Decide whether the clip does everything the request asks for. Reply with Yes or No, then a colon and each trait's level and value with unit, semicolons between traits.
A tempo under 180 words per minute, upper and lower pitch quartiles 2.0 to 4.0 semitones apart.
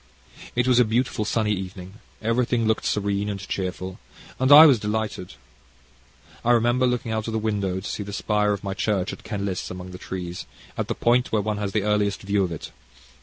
No: fast, 205 wpm; average, 2.8 semitones